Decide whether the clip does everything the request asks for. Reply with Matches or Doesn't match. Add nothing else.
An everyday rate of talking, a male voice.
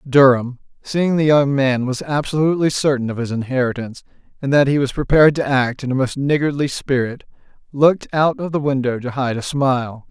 Matches